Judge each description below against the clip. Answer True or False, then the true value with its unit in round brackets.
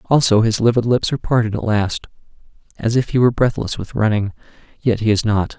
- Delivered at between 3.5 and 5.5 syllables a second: False (6.0 syllables/s)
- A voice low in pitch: True (115 Hz)